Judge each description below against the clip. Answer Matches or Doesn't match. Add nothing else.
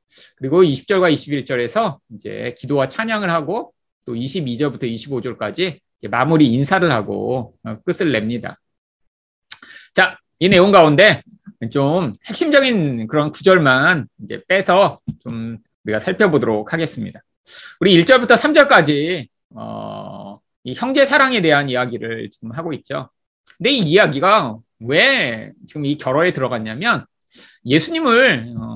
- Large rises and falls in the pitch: Matches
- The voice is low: Doesn't match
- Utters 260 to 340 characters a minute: Matches